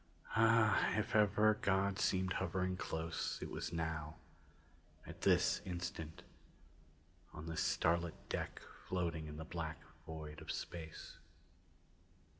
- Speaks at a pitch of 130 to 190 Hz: No, very low, 85 Hz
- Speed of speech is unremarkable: No, slow, 115 wpm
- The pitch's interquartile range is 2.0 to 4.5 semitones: Yes, average, 3.1 semitones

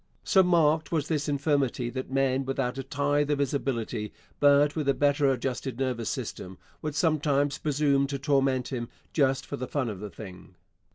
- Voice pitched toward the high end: No, medium, 140 Hz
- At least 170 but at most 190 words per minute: Yes, average, 180 wpm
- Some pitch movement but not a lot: No, narrow, 2.2 semitones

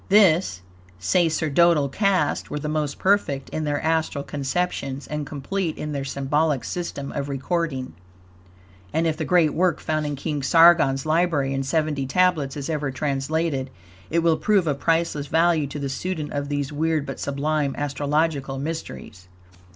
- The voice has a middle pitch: Yes, medium, 150 Hz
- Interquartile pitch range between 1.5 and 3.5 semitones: Yes, average, 2.9 semitones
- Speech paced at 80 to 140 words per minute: No, average, 155 wpm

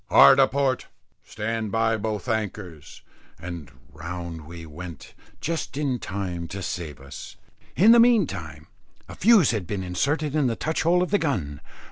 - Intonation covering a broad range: Yes, wide, 8.7 semitones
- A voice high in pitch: No, low, 105 Hz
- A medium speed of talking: Yes, average, 160 wpm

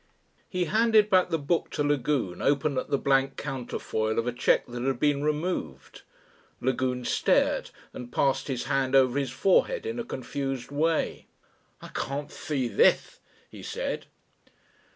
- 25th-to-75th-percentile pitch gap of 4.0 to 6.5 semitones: No, average, 3.1 semitones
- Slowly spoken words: No, average, 150 wpm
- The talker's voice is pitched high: No, medium, 140 Hz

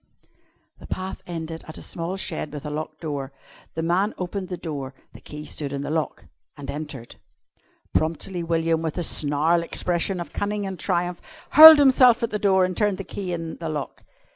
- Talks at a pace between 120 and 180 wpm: No, average, 190 wpm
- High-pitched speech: No, medium, 170 Hz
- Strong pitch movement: No, average, 3.6 semitones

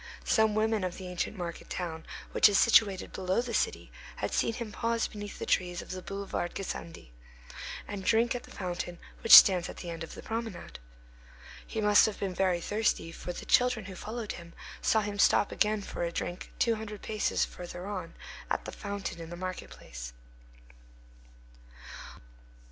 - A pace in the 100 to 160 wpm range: No, average, 180 wpm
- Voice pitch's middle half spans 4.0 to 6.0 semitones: No, average, 3.5 semitones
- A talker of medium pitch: No, high, 195 Hz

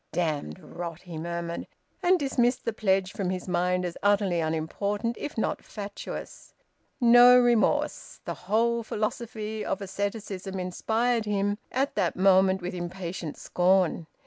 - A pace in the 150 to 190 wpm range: No, average, 140 wpm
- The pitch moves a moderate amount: Yes, average, 3.8 semitones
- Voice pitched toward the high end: Yes, high, 195 Hz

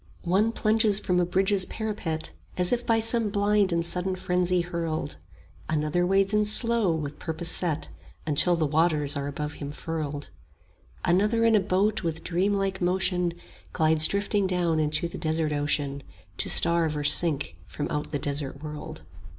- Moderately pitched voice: Yes, medium, 175 Hz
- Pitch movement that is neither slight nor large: Yes, average, 4.1 semitones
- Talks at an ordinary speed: Yes, average, 165 wpm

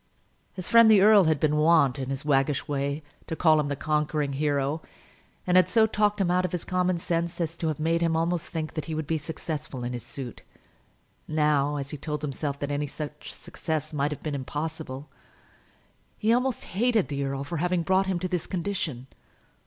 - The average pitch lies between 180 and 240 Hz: No, medium, 155 Hz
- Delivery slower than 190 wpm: No, fast, 205 wpm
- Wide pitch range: No, average, 3.6 semitones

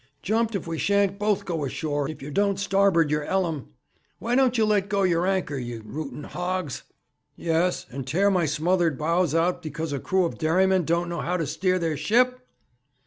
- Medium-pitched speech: Yes, medium, 175 Hz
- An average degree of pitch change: Yes, average, 3.9 semitones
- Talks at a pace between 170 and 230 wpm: Yes, average, 195 wpm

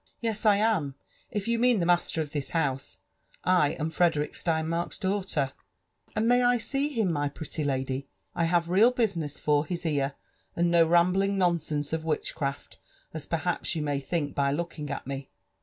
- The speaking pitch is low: No, medium, 165 Hz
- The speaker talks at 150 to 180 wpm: No, average, 200 wpm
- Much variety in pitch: No, average, 4.7 semitones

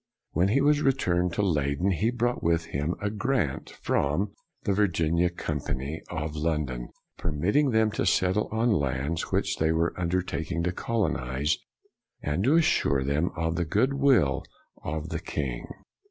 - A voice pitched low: Yes, very low, 85 Hz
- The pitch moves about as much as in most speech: No, wide, 5.9 semitones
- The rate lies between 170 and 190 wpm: No, average, 155 wpm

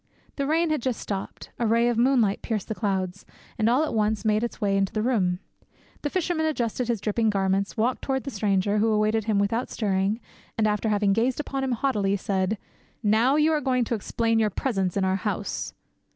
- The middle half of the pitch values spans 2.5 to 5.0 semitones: Yes, average, 3.7 semitones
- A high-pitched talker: Yes, high, 220 Hz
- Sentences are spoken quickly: Yes, fast, 210 wpm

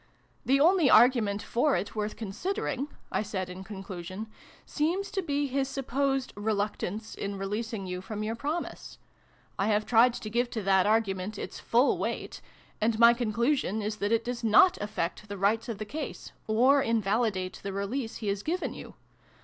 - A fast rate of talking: No, average, 180 wpm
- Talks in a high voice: Yes, high, 220 Hz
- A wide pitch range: No, average, 4.1 semitones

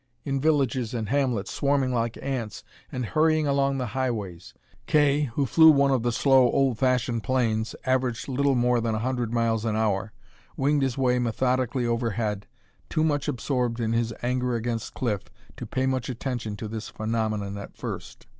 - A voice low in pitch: Yes, low, 125 Hz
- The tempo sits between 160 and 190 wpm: Yes, average, 175 wpm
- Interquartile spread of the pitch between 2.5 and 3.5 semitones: Yes, average, 2.9 semitones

